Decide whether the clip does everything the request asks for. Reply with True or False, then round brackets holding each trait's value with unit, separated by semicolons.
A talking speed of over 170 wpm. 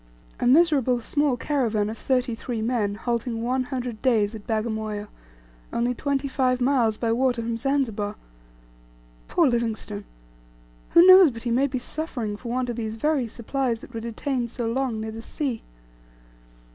False (160 wpm)